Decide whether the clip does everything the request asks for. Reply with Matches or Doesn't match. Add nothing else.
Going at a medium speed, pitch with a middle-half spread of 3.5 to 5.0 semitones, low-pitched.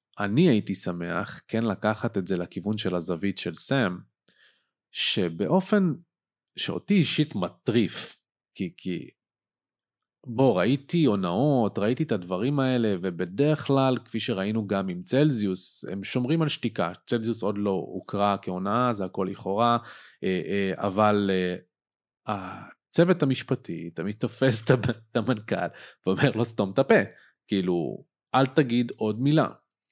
Doesn't match